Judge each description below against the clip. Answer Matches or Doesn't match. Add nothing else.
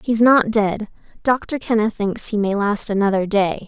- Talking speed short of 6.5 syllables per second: Matches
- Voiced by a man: Doesn't match